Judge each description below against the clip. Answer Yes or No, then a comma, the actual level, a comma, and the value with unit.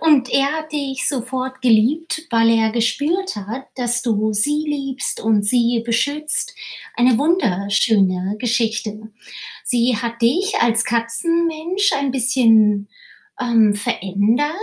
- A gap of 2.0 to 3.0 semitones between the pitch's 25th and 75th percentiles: No, average, 4.6 semitones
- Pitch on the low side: No, high, 240 Hz